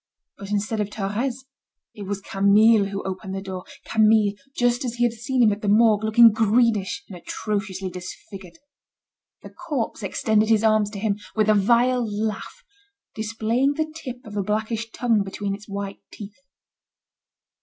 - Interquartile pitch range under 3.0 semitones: Yes, narrow, 2.4 semitones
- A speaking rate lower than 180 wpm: Yes, average, 165 wpm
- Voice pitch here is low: No, high, 215 Hz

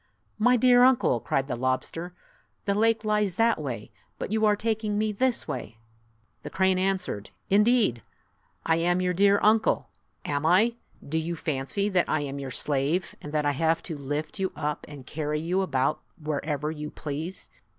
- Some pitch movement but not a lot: No, wide, 6.0 semitones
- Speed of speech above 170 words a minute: Yes, average, 180 wpm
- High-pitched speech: No, medium, 170 Hz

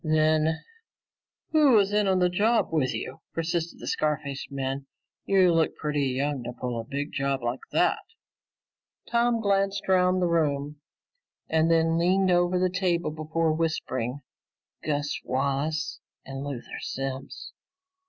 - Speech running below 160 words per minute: Yes, average, 145 wpm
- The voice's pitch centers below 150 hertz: No, medium, 155 Hz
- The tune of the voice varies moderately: Yes, average, 4.5 semitones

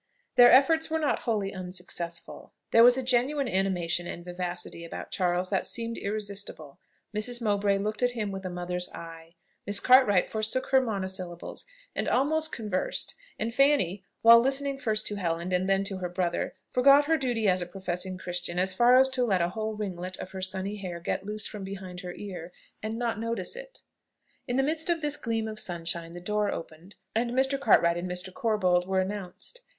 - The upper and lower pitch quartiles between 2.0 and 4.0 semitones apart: No, average, 5.0 semitones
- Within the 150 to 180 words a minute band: No, average, 190 wpm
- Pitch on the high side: Yes, high, 200 Hz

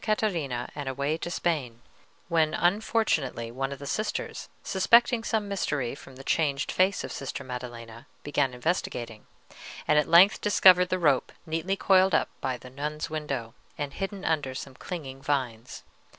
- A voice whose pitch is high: No, medium, 145 Hz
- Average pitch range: No, wide, 5.7 semitones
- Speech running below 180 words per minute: Yes, average, 155 wpm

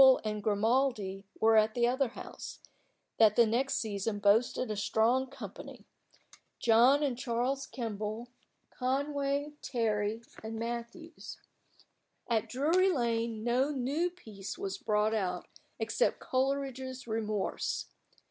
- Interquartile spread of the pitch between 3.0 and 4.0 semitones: Yes, average, 3.6 semitones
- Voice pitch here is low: No, high, 235 Hz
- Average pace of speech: No, slow, 120 wpm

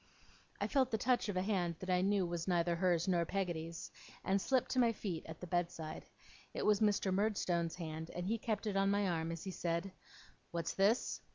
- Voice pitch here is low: No, medium, 185 Hz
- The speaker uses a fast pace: Yes, fast, 215 wpm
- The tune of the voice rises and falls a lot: No, average, 3.3 semitones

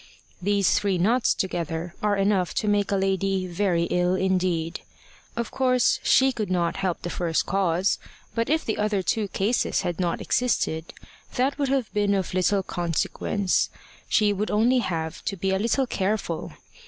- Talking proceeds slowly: No, average, 165 wpm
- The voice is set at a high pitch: Yes, high, 195 Hz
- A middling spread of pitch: Yes, average, 3.2 semitones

